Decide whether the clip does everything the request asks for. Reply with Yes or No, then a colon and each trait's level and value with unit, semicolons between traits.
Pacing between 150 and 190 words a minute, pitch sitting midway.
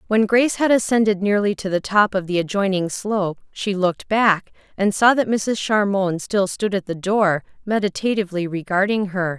No: average, 180 wpm; high, 200 Hz